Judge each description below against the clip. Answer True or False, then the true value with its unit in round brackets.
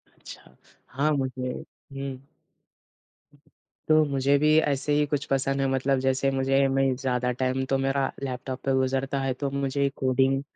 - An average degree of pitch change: False (0.9 semitones)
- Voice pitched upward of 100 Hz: True (135 Hz)